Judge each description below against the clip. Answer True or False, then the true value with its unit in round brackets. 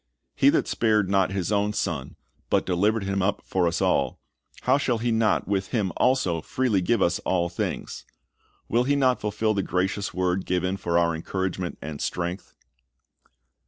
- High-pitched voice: False (95 Hz)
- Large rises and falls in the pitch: False (3.4 semitones)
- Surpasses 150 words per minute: True (170 wpm)